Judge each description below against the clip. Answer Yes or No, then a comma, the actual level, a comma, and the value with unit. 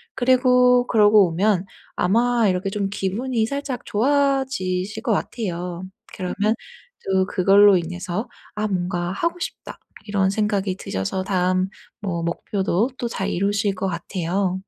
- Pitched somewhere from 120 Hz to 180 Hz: No, high, 200 Hz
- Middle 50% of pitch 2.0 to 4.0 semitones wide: Yes, average, 3.7 semitones